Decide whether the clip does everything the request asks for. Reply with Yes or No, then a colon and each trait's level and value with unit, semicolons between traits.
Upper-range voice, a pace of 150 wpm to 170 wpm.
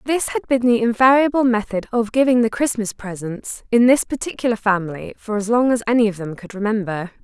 No: high, 225 Hz; average, 200 wpm